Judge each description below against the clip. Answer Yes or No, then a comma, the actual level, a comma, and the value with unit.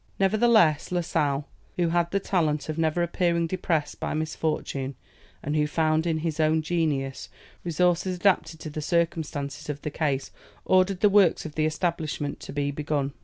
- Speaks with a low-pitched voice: No, medium, 160 Hz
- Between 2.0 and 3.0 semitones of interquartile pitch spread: Yes, average, 2.7 semitones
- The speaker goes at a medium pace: Yes, average, 170 wpm